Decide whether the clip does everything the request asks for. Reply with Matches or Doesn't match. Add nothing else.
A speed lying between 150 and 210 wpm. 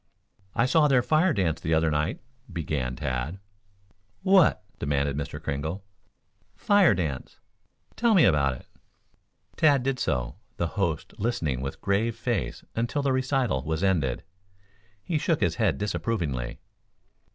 Doesn't match